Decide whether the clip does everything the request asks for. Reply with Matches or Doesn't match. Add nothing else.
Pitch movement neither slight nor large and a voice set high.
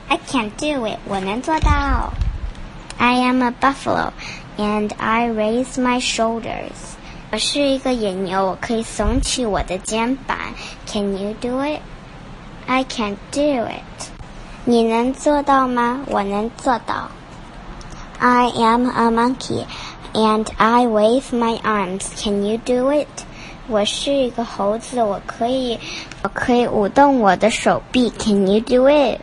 Matches